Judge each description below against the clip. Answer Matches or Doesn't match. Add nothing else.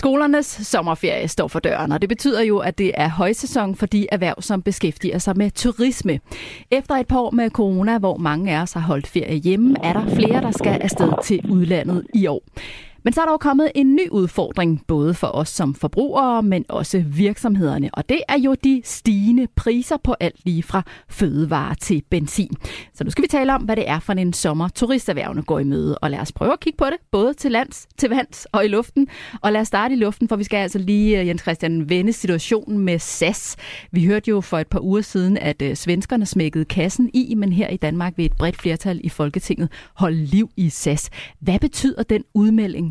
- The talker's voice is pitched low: Doesn't match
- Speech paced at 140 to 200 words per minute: Doesn't match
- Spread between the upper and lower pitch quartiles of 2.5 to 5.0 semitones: Doesn't match